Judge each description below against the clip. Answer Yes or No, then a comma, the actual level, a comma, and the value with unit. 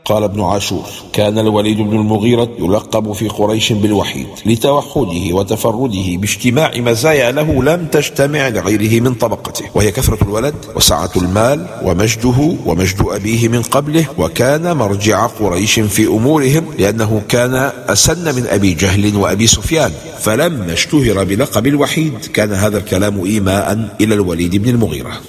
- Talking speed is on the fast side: No, slow, 135 wpm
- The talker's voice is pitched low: Yes, low, 110 Hz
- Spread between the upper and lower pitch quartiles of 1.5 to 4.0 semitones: No, average, 4.4 semitones